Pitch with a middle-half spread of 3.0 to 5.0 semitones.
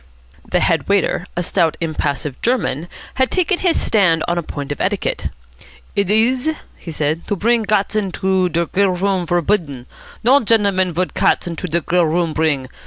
Yes: average, 4.1 semitones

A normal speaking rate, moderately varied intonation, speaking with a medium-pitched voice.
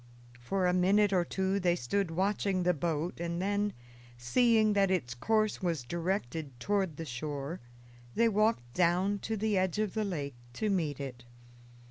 Yes: average, 165 wpm; average, 4.7 semitones; medium, 180 Hz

